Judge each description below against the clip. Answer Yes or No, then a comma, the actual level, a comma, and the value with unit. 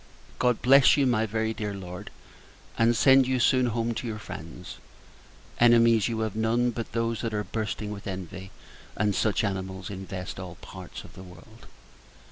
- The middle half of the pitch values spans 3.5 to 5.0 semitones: No, average, 2.9 semitones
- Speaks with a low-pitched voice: Yes, low, 110 Hz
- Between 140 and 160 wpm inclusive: No, average, 170 wpm